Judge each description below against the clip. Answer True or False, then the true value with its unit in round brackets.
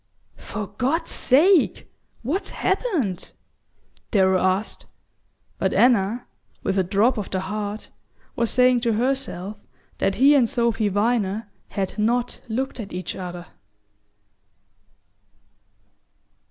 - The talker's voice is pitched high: True (220 Hz)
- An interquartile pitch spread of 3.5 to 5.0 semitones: True (4.4 semitones)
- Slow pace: True (110 wpm)